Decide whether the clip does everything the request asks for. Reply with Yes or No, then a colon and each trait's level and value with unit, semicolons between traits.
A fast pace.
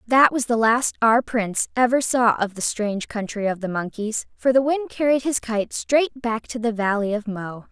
Yes: fast, 220 wpm